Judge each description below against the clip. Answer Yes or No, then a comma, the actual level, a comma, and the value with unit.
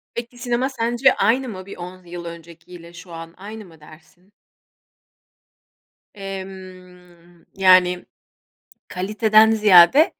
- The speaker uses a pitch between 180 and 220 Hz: Yes, medium, 185 Hz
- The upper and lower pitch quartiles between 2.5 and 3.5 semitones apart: No, average, 3.9 semitones